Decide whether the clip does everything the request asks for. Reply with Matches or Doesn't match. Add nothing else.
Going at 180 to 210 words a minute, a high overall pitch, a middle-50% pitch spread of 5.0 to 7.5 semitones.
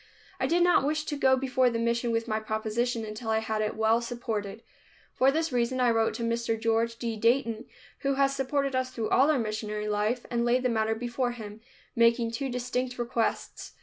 Doesn't match